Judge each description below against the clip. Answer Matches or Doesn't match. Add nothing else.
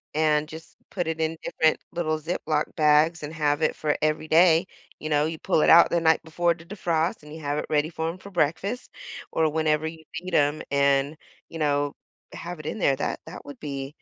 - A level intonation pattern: Matches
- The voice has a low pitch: Doesn't match